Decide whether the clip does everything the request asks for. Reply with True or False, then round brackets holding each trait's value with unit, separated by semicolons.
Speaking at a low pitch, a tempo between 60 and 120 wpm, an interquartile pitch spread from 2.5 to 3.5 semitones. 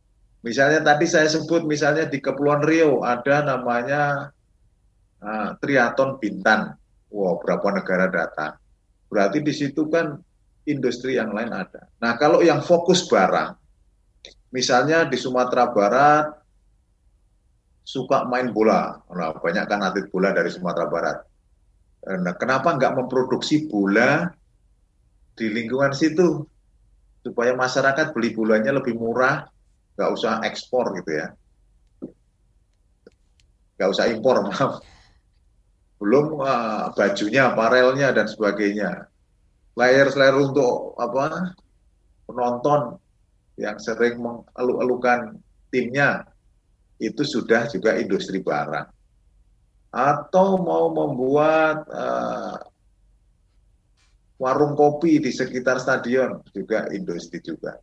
False (130 Hz; 105 wpm; 4.2 semitones)